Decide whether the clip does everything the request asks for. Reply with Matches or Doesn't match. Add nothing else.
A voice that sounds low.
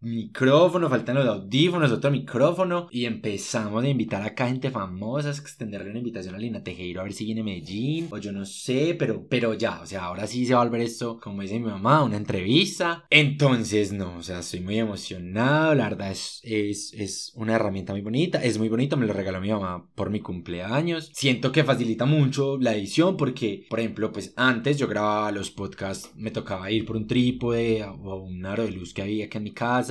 Matches